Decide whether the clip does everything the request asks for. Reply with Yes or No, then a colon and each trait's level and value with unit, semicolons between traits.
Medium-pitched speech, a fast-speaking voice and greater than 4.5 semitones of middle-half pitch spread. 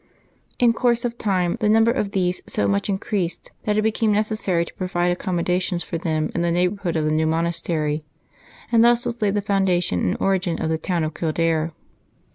No: medium, 180 Hz; fast, 210 wpm; average, 4.0 semitones